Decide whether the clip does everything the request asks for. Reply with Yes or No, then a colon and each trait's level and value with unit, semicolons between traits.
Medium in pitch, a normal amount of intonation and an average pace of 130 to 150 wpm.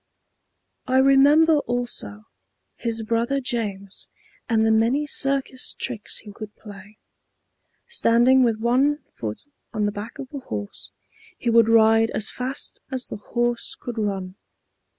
No: high, 230 Hz; average, 3.5 semitones; slow, 135 wpm